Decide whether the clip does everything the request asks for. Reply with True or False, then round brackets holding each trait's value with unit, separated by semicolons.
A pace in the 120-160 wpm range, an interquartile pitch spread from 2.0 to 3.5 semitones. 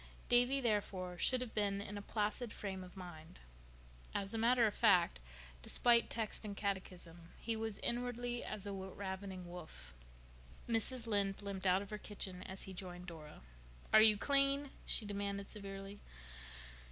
True (155 wpm; 3.1 semitones)